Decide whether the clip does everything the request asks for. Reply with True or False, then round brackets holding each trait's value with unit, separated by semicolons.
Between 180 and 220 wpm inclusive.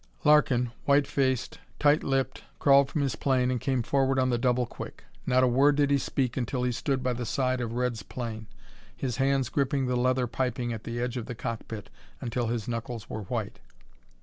True (200 wpm)